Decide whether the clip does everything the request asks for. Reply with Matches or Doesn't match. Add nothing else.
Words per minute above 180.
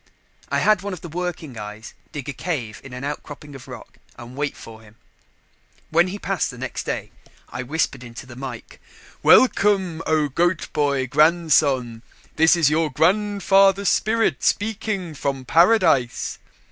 Doesn't match